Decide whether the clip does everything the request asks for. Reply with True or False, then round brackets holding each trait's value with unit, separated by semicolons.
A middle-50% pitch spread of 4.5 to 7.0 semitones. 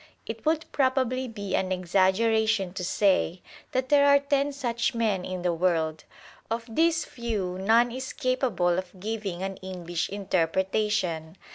True (5.2 semitones)